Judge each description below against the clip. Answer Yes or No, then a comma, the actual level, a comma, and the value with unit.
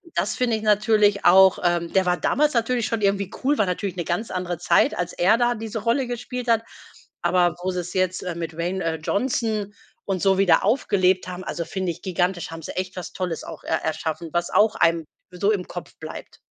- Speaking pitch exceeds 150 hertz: Yes, high, 190 Hz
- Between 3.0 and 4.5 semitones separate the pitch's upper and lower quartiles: Yes, average, 3.6 semitones